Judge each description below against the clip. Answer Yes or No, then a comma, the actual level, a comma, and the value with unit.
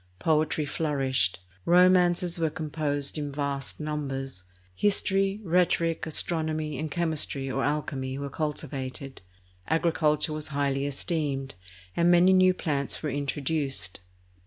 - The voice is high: No, medium, 150 Hz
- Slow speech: Yes, slow, 115 wpm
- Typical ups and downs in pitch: Yes, average, 3.1 semitones